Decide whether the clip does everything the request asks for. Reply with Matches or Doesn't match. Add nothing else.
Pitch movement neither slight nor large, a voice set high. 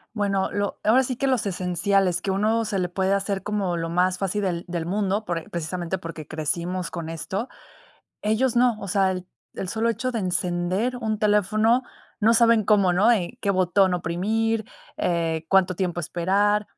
Matches